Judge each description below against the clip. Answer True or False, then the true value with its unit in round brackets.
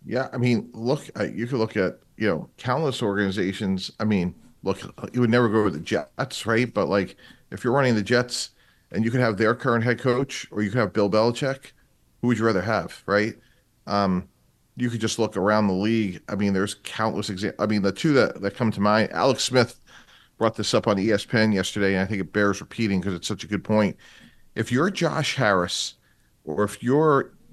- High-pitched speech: False (110 Hz)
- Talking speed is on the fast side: True (215 wpm)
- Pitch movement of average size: True (3.2 semitones)